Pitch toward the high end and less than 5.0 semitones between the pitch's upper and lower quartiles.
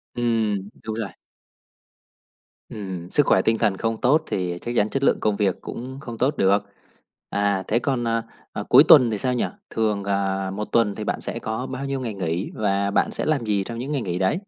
No: low, 110 Hz; average, 3.5 semitones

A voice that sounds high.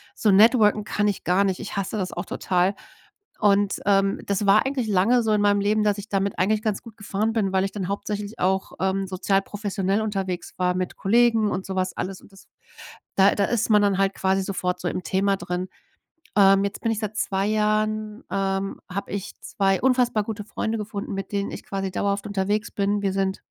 Yes: high, 200 Hz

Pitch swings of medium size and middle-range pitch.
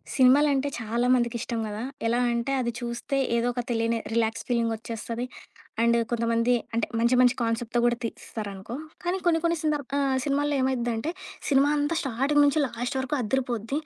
No: average, 3.0 semitones; high, 240 Hz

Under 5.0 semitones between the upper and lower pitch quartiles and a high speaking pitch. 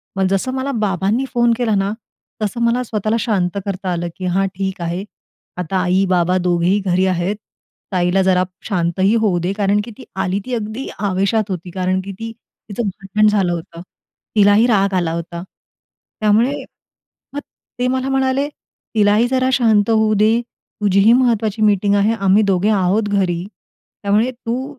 Yes: average, 3.3 semitones; high, 200 Hz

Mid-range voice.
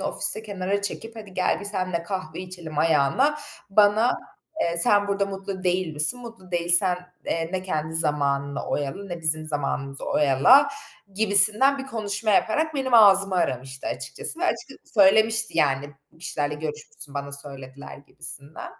Yes: medium, 180 Hz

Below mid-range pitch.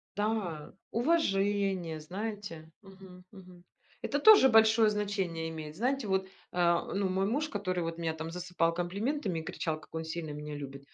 No: medium, 185 Hz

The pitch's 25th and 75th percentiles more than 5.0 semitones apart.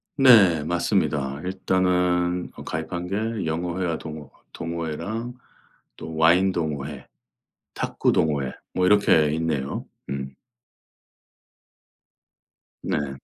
No: average, 3.3 semitones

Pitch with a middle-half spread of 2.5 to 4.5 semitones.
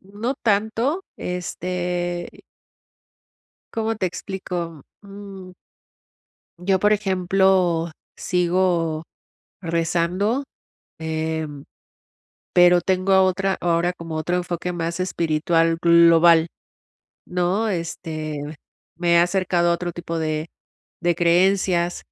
No: narrow, 2.1 semitones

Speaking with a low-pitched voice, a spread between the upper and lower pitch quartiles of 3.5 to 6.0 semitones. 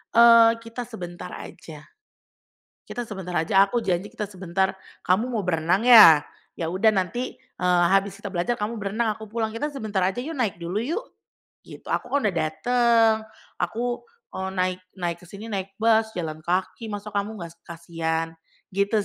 No: high, 200 Hz; average, 4.2 semitones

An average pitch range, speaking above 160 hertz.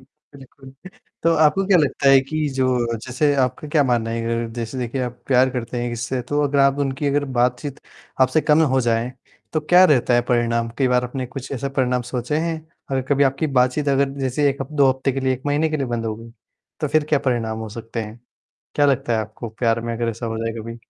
No: average, 3.3 semitones; low, 130 Hz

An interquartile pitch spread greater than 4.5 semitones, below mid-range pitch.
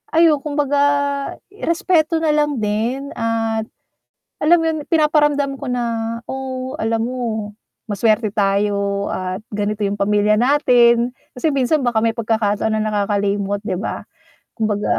No: average, 5.1 semitones; high, 230 Hz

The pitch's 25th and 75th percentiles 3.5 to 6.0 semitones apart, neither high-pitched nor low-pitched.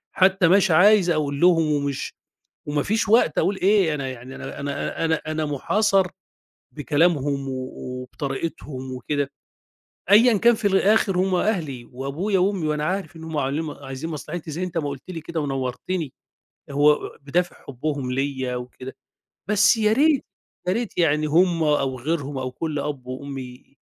Yes: average, 5.1 semitones; medium, 155 Hz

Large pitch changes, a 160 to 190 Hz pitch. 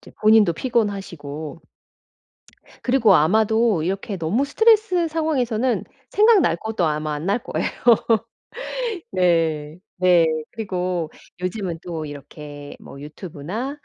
Yes: wide, 6.3 semitones; medium, 185 Hz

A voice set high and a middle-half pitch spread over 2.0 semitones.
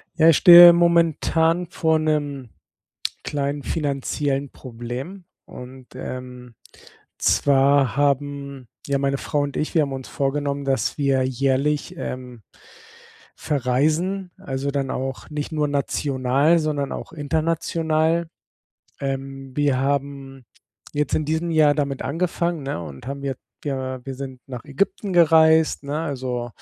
No: medium, 140 Hz; average, 2.8 semitones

